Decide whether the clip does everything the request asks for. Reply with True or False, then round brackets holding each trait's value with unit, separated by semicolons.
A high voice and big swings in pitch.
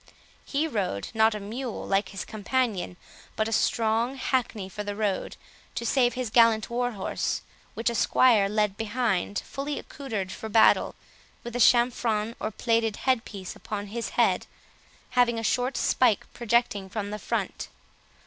False (225 Hz; 2.8 semitones)